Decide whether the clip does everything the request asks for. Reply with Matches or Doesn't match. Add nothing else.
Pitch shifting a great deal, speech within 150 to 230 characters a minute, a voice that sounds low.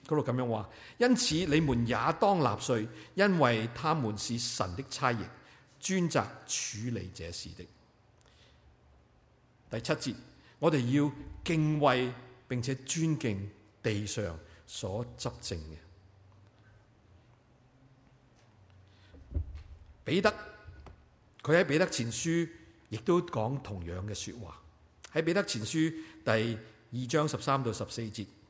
Matches